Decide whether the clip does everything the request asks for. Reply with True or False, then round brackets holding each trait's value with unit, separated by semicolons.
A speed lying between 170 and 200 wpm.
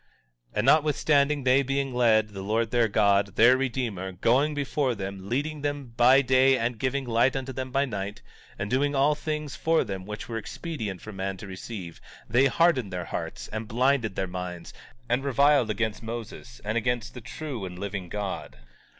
True (185 wpm)